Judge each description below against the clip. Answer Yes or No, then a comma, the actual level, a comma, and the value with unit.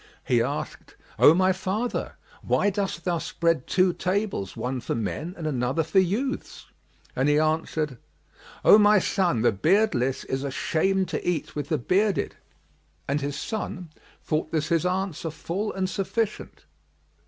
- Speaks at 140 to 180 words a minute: Yes, average, 150 wpm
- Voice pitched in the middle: Yes, medium, 170 Hz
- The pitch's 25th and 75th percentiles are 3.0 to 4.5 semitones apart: No, average, 4.9 semitones